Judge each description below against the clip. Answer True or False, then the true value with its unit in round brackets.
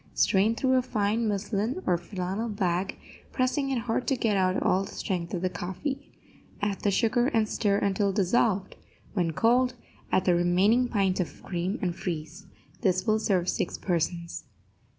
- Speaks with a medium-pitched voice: False (200 Hz)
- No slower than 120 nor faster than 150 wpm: False (170 wpm)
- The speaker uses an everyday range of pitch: True (3.9 semitones)